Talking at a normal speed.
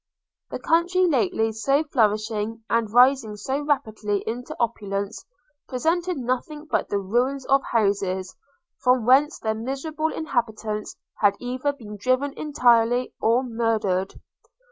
No: slow, 120 wpm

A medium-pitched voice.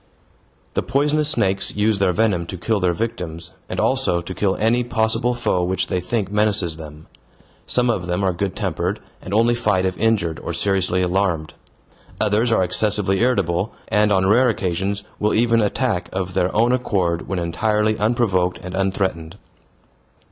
No: low, 100 Hz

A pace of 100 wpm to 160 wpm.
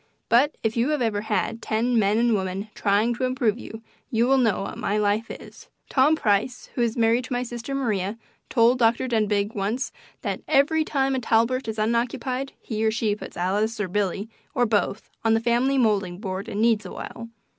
No: average, 190 wpm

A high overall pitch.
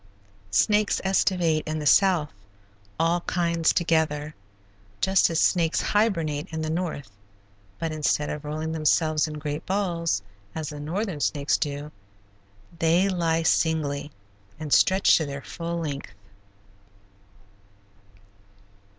No: medium, 160 Hz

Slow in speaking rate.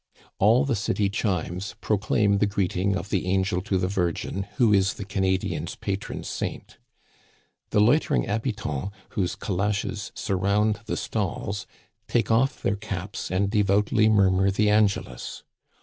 No: average, 150 wpm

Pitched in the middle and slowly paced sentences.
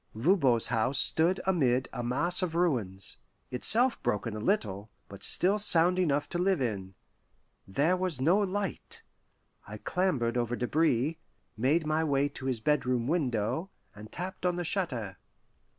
No: medium, 145 Hz; average, 150 wpm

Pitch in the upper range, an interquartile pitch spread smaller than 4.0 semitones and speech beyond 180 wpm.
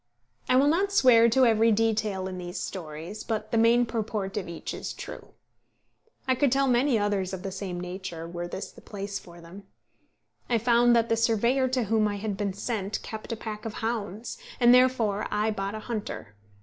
Yes: high, 215 Hz; average, 3.4 semitones; average, 200 wpm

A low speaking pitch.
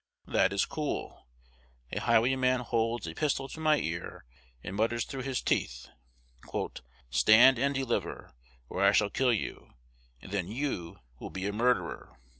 Yes: low, 115 Hz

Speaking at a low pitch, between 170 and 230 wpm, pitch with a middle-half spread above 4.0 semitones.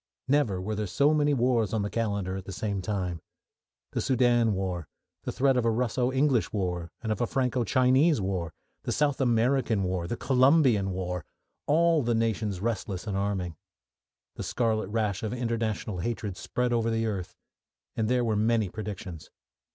Yes: low, 110 Hz; average, 175 wpm; average, 4.4 semitones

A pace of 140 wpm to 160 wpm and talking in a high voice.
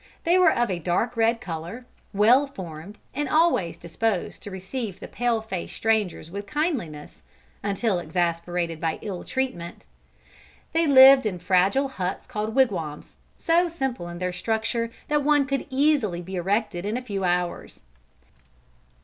Yes: average, 150 wpm; high, 210 Hz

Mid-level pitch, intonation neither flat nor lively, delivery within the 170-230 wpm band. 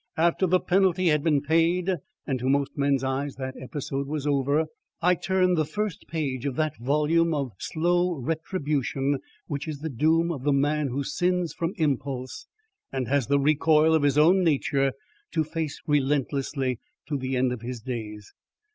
Yes: medium, 145 Hz; average, 3.3 semitones; average, 175 wpm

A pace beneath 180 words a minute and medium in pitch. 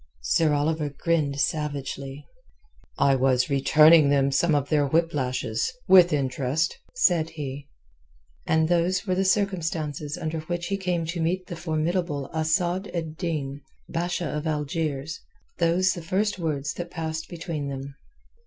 Yes: average, 140 wpm; medium, 160 Hz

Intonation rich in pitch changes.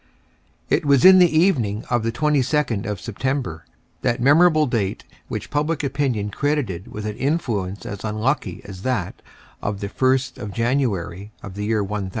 Yes: wide, 5.7 semitones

